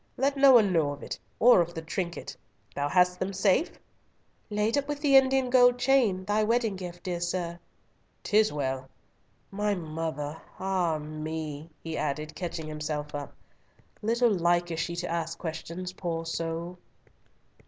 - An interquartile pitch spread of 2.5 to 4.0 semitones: No, average, 4.7 semitones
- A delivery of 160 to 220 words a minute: No, average, 150 wpm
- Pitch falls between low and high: Yes, medium, 175 Hz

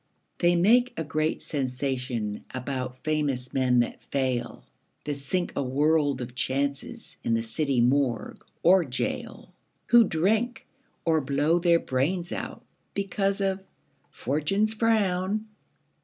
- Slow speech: Yes, slow, 125 wpm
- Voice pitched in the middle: Yes, medium, 150 Hz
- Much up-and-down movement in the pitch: Yes, wide, 6.2 semitones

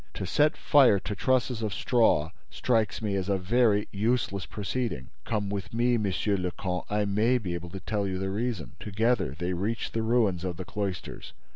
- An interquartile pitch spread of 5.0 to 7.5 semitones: No, average, 3.5 semitones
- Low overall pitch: Yes, low, 105 Hz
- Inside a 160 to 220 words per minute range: Yes, average, 190 wpm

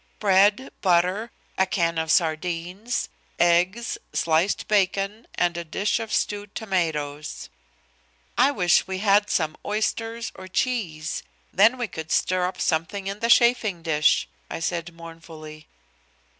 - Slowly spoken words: Yes, slow, 130 wpm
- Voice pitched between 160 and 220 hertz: Yes, medium, 185 Hz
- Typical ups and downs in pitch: Yes, average, 4.0 semitones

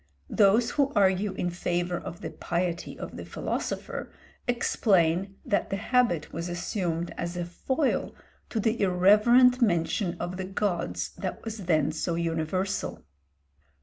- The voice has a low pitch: No, medium, 185 Hz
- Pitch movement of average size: Yes, average, 3.6 semitones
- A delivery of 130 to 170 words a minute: Yes, average, 140 wpm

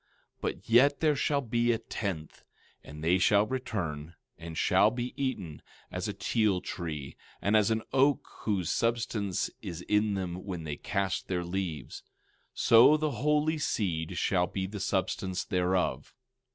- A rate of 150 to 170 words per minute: Yes, average, 155 wpm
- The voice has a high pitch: No, low, 100 Hz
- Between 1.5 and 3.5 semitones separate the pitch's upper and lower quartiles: No, average, 5.1 semitones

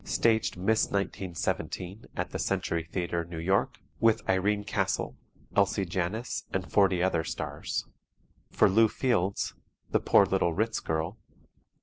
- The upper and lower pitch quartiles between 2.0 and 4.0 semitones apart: Yes, average, 3.2 semitones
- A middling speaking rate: No, slow, 130 wpm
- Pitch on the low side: Yes, very low, 95 Hz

